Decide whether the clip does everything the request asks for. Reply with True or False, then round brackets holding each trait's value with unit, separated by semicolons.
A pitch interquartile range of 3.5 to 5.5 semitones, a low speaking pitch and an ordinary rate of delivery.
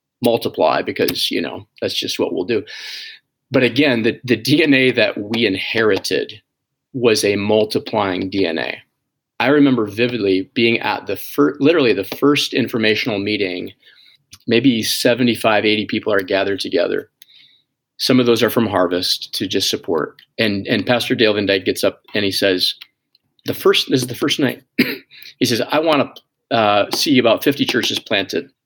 True (3.9 semitones; 115 Hz; 165 wpm)